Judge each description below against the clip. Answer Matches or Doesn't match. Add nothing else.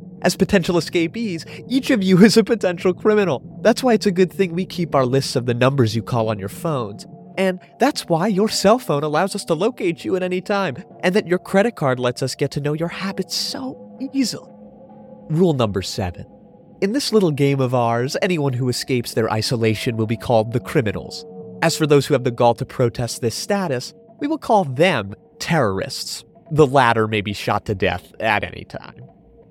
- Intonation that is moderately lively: Doesn't match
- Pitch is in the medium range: Matches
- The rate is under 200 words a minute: Doesn't match